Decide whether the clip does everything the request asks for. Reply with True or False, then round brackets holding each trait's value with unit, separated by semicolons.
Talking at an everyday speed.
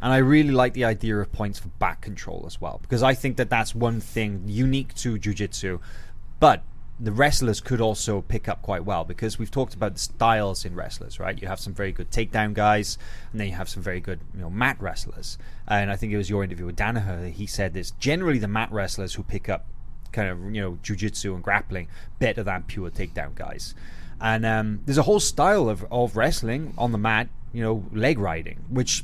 False (220 wpm)